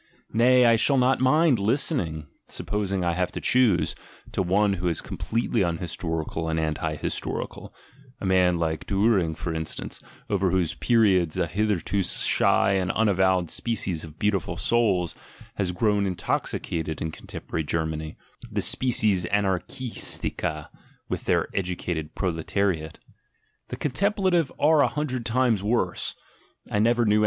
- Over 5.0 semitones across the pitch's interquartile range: Yes, wide, 5.5 semitones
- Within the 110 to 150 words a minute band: Yes, average, 145 wpm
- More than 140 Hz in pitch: No, very low, 95 Hz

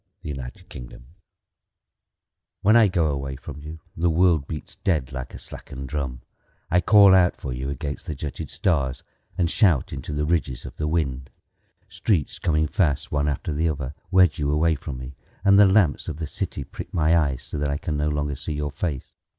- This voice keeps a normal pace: Yes, average, 195 wpm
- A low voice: Yes, very low, 75 Hz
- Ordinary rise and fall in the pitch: Yes, average, 3.3 semitones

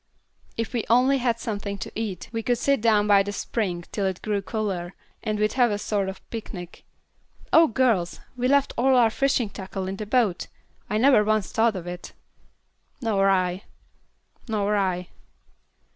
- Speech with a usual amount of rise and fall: Yes, average, 3.3 semitones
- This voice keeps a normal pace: Yes, average, 175 wpm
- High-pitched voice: Yes, high, 210 Hz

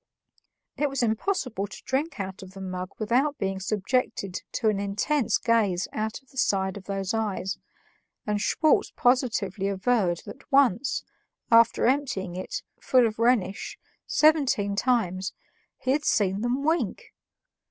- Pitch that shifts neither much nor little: Yes, average, 4.9 semitones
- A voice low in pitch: No, high, 220 Hz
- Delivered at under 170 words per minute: Yes, average, 140 wpm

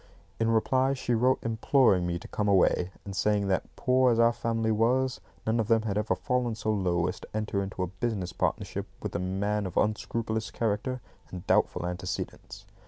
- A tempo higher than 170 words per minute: Yes, average, 190 wpm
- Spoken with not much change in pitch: No, average, 3.3 semitones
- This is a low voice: Yes, low, 110 Hz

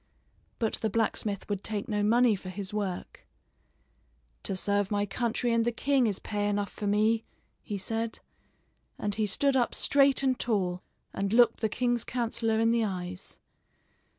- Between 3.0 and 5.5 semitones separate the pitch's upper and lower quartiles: No, narrow, 2.6 semitones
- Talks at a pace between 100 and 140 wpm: No, average, 165 wpm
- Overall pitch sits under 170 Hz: No, high, 215 Hz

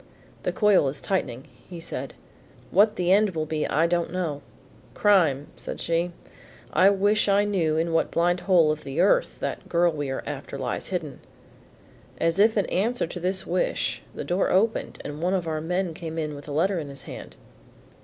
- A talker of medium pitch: Yes, medium, 175 Hz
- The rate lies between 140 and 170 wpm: No, average, 195 wpm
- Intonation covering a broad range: No, average, 3.9 semitones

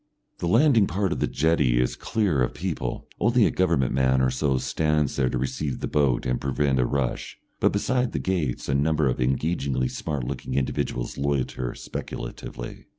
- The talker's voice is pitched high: No, very low, 70 Hz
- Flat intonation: No, average, 4.6 semitones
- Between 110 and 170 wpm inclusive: No, average, 180 wpm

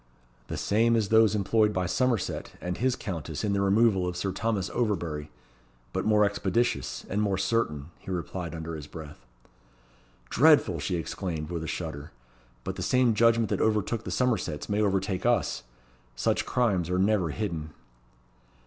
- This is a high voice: No, very low, 95 Hz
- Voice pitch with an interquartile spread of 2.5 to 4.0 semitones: No, average, 4.7 semitones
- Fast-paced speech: No, average, 160 wpm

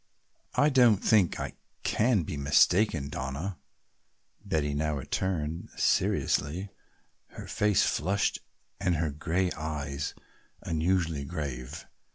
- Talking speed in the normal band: No, slow, 105 wpm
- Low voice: Yes, very low, 80 Hz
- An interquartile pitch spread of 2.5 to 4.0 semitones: No, average, 4.6 semitones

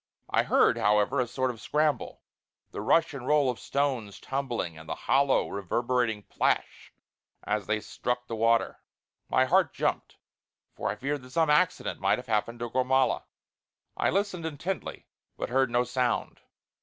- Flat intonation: No, average, 3.7 semitones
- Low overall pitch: Yes, low, 125 Hz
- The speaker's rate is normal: Yes, average, 160 wpm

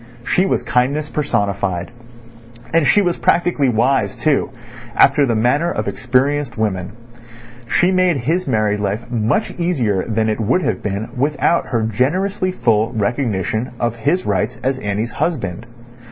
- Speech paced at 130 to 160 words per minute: Yes, average, 145 wpm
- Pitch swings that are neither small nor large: No, wide, 5.8 semitones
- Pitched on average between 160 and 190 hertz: No, low, 125 Hz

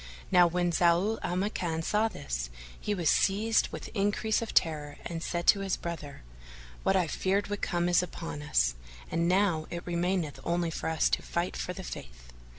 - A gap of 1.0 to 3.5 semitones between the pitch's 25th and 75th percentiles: Yes, average, 3.0 semitones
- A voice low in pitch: No, medium, 175 Hz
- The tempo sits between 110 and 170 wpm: No, average, 190 wpm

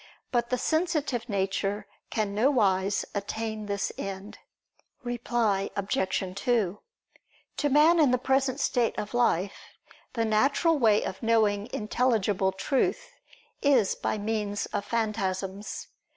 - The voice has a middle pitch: No, high, 220 Hz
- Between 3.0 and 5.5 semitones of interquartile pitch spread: Yes, average, 4.0 semitones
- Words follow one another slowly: Yes, slow, 120 wpm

